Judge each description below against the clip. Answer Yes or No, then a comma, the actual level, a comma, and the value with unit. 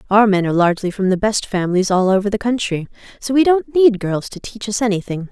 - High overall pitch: Yes, high, 205 Hz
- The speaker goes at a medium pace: No, fast, 235 wpm